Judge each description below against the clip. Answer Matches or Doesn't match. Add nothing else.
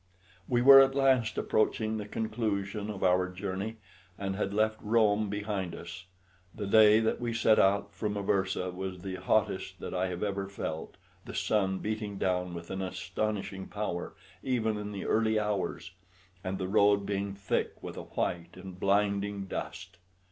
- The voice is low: Matches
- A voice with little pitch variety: Matches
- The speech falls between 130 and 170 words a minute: Matches